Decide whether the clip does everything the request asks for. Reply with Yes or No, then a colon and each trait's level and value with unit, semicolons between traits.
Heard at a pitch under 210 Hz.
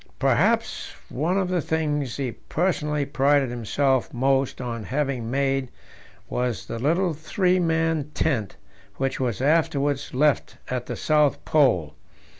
Yes: medium, 140 Hz